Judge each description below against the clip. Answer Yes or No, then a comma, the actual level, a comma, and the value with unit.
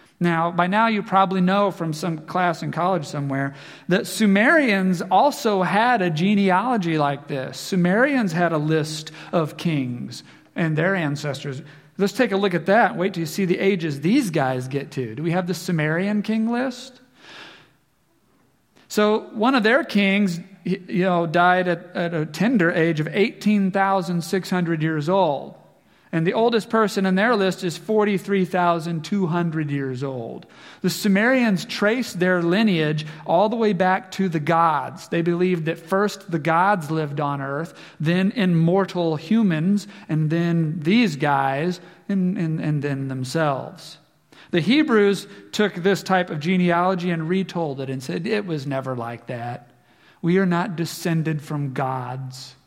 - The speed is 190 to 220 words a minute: No, average, 155 wpm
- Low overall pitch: No, medium, 175 Hz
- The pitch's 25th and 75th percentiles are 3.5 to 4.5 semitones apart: Yes, average, 3.8 semitones